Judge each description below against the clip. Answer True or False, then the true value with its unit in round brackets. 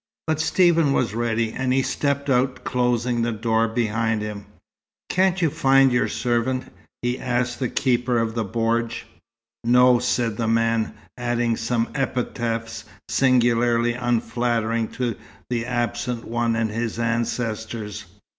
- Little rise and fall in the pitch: True (1.5 semitones)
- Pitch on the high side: False (120 Hz)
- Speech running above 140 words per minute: False (135 wpm)